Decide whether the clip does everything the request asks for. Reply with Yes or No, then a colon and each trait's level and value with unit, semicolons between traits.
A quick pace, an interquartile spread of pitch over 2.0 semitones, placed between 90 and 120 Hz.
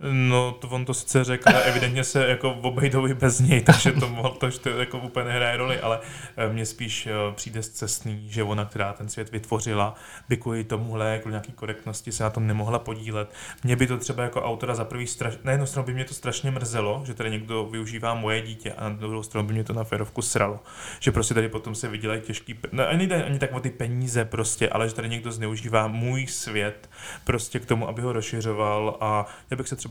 Yes: fast, 225 wpm; narrow, 2.6 semitones; low, 115 Hz